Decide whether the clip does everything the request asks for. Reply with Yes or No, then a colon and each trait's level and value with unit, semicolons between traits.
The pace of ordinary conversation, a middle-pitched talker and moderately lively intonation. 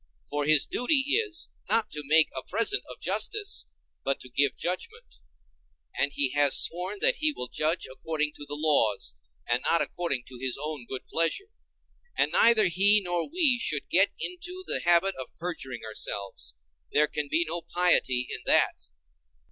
No: average, 165 wpm; medium, 155 Hz; wide, 7.3 semitones